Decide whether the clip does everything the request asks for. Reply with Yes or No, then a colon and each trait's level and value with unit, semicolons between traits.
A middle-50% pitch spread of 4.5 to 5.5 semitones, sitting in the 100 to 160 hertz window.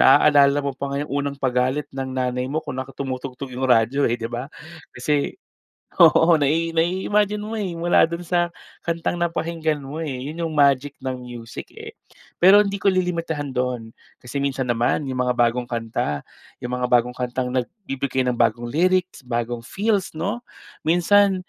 Yes: average, 5.0 semitones; medium, 140 Hz